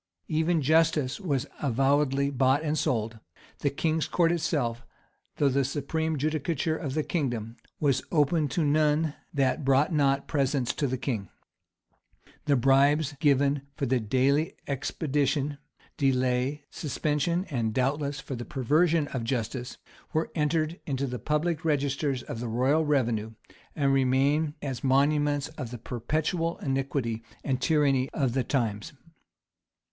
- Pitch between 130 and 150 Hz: Yes, medium, 140 Hz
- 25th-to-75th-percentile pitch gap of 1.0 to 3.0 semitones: Yes, average, 2.7 semitones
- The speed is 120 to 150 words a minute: Yes, slow, 135 wpm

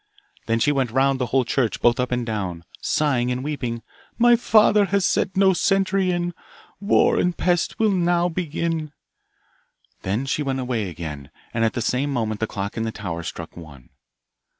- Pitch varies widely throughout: Yes, wide, 7.7 semitones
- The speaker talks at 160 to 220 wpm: Yes, average, 180 wpm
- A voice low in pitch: Yes, low, 130 Hz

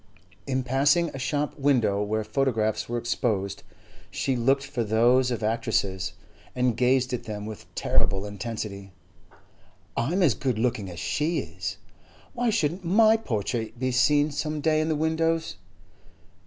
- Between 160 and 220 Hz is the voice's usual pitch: No, low, 125 Hz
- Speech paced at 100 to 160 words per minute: Yes, average, 150 wpm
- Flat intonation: No, average, 5.3 semitones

